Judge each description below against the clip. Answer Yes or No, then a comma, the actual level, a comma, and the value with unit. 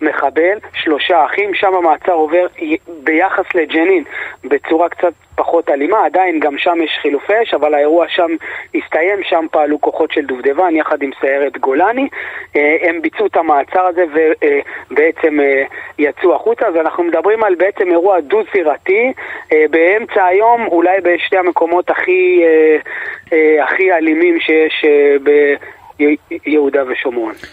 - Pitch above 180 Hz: No, medium, 175 Hz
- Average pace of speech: Yes, average, 125 wpm